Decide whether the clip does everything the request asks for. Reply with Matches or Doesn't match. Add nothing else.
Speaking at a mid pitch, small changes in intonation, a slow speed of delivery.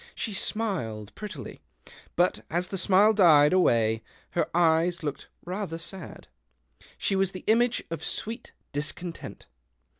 Doesn't match